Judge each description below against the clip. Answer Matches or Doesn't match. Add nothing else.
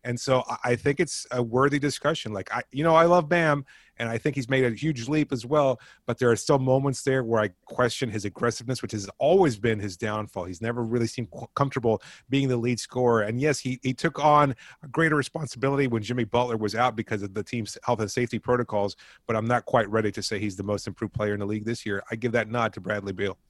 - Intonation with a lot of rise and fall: Doesn't match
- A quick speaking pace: Matches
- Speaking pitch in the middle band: Doesn't match